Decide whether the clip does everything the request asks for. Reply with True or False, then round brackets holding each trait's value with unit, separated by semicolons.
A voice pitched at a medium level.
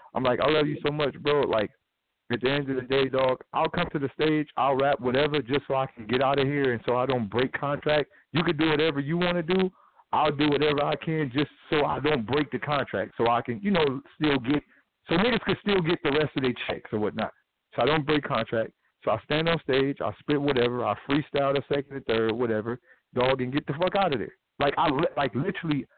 True (145 Hz)